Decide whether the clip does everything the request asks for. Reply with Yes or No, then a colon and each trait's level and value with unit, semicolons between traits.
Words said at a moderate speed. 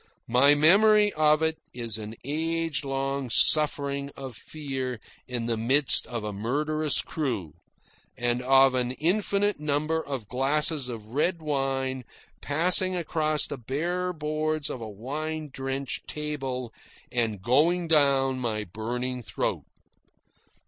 No: slow, 130 wpm